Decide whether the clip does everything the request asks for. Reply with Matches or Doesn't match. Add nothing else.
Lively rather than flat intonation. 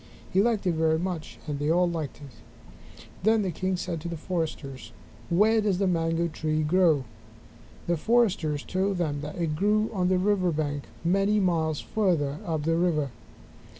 Doesn't match